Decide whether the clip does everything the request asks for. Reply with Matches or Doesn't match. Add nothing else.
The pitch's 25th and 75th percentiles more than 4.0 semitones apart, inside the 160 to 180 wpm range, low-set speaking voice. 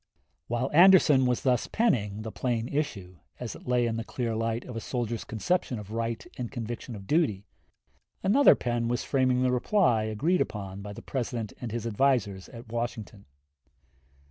Doesn't match